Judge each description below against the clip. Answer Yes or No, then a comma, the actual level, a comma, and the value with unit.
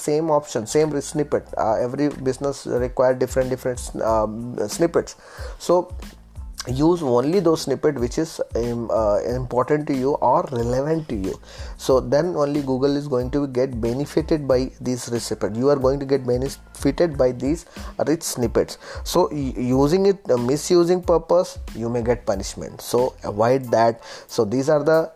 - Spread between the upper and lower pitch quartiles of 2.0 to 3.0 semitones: No, average, 3.4 semitones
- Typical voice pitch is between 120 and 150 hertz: Yes, low, 135 Hz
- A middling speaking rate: No, fast, 160 wpm